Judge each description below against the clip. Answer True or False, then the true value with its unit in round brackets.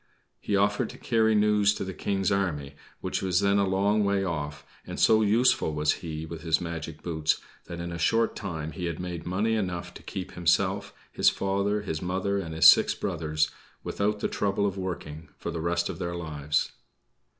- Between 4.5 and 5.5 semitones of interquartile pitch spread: False (3.8 semitones)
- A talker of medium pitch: False (90 Hz)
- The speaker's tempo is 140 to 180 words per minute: False (195 wpm)